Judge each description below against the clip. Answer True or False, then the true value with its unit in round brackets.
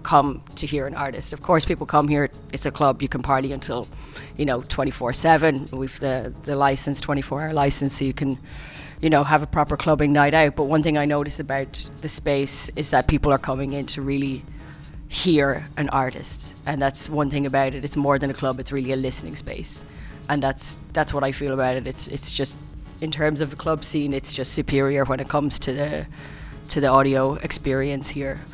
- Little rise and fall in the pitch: True (1.6 semitones)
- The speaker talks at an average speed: False (210 wpm)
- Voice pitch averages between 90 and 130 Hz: False (140 Hz)